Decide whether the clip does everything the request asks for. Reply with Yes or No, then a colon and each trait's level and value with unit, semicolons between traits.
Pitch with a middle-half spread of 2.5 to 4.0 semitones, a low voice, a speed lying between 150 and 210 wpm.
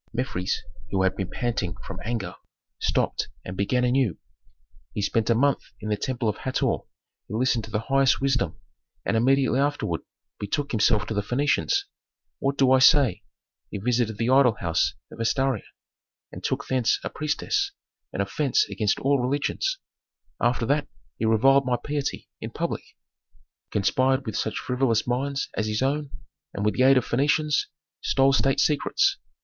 Yes: average, 3.7 semitones; low, 125 Hz; average, 165 wpm